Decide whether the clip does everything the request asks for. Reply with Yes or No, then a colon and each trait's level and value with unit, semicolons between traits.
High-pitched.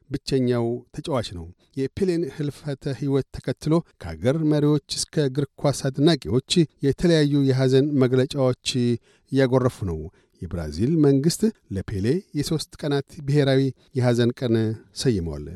No: low, 135 Hz